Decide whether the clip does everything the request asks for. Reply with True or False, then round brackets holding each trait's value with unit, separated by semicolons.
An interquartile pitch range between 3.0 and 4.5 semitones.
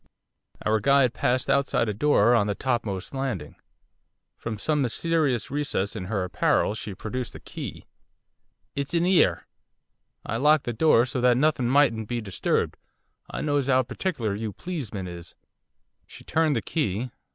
False (4.9 semitones)